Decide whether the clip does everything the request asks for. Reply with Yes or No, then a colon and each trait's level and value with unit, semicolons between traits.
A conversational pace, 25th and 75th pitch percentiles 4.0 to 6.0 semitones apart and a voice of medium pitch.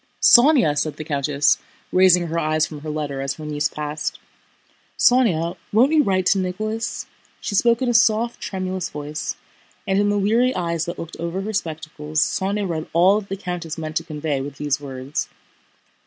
Yes: average, 185 wpm; average, 5.0 semitones; medium, 170 Hz